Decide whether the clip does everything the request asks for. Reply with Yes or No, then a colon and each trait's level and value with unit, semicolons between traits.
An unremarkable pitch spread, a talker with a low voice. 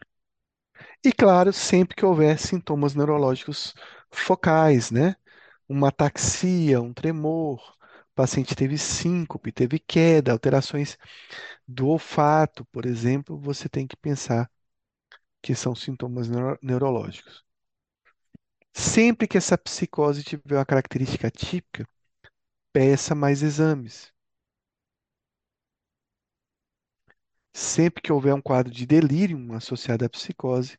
No: average, 3.6 semitones; medium, 145 Hz